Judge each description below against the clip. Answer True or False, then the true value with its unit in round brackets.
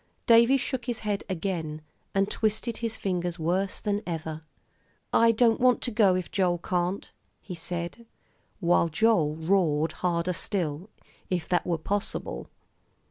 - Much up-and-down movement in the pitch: False (4.4 semitones)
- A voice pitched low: False (185 Hz)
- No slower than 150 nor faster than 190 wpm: False (140 wpm)